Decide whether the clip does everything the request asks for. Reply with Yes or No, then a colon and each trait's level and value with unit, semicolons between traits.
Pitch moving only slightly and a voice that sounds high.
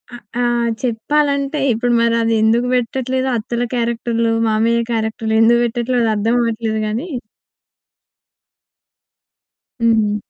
Yes: narrow, 1.4 semitones; high, 235 Hz